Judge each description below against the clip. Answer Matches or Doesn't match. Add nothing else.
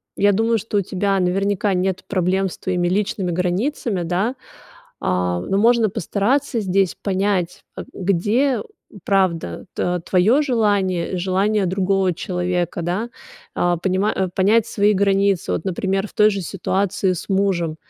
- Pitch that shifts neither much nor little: Doesn't match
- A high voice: Matches